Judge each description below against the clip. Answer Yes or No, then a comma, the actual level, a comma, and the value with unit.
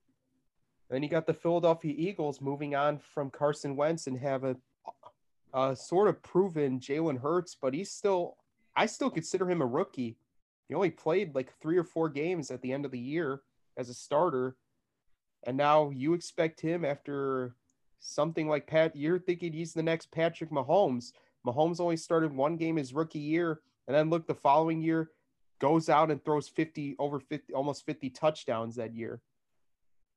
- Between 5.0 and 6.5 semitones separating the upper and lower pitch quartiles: No, average, 3.7 semitones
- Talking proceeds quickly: No, average, 175 wpm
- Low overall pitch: No, medium, 150 Hz